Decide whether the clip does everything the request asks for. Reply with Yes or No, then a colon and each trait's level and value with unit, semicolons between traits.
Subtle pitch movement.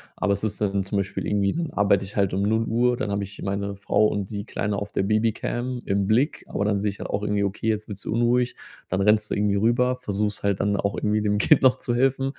Yes: narrow, 2.3 semitones